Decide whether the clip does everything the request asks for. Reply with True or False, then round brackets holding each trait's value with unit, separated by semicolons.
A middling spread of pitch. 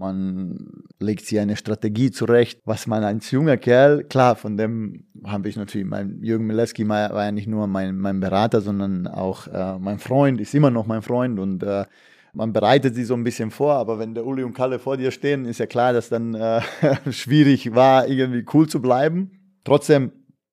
True (3.9 semitones)